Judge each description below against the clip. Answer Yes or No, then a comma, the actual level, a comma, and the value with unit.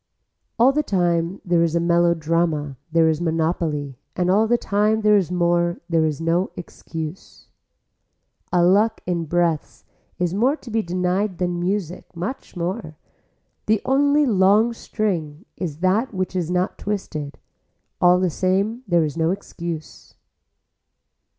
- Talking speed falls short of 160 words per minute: Yes, average, 145 wpm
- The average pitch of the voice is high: No, medium, 175 Hz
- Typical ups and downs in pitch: Yes, average, 3.4 semitones